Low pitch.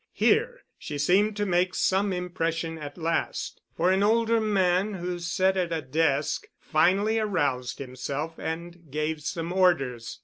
No: medium, 175 Hz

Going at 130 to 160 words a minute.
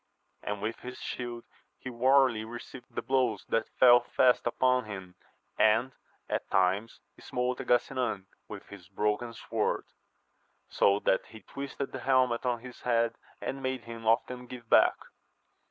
Yes: average, 150 wpm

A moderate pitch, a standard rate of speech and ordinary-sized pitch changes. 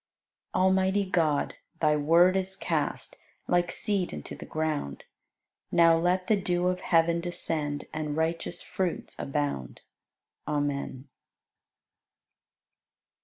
No: medium, 170 Hz; slow, 110 wpm; average, 3.4 semitones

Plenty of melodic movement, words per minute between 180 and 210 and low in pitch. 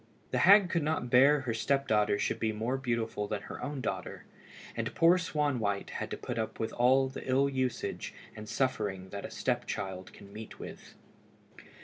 No: average, 4.3 semitones; average, 190 wpm; low, 125 Hz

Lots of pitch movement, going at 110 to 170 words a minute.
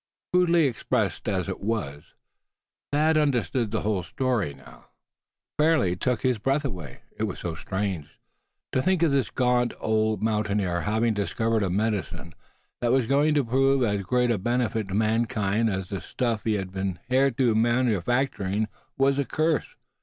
No: average, 4.6 semitones; average, 160 wpm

